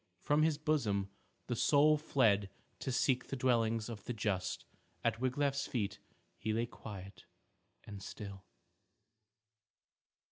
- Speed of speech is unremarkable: No, slow, 120 wpm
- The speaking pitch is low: Yes, low, 115 Hz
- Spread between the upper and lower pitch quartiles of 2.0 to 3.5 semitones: No, average, 5.0 semitones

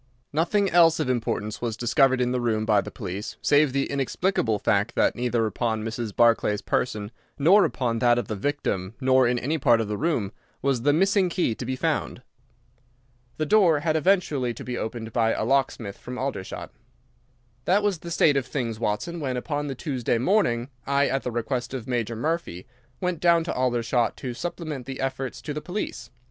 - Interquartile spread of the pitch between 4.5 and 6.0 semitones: Yes, average, 4.8 semitones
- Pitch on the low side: Yes, low, 130 Hz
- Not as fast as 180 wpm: No, average, 190 wpm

